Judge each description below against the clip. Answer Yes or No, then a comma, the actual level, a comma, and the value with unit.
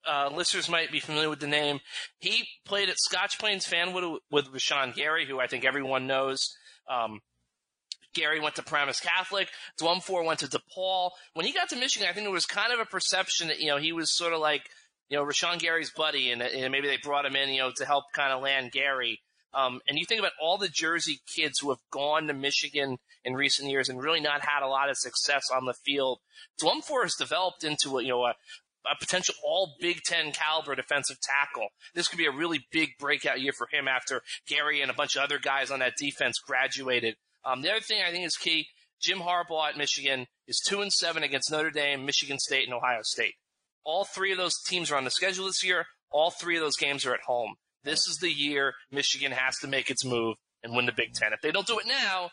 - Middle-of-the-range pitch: Yes, medium, 150 Hz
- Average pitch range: Yes, average, 4.3 semitones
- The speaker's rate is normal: No, fast, 235 wpm